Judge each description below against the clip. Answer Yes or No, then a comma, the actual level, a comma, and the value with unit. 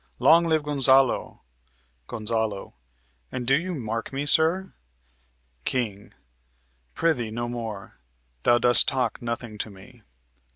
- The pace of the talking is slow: Yes, slow, 115 wpm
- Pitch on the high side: No, low, 120 Hz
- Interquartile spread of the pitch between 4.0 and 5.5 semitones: Yes, average, 4.5 semitones